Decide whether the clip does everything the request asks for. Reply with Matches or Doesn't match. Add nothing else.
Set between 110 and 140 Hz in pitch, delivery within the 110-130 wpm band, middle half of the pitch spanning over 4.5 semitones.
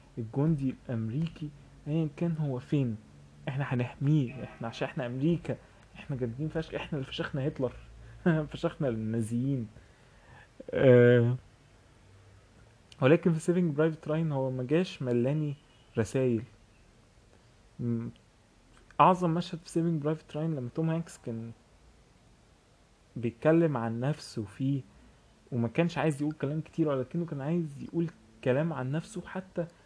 Matches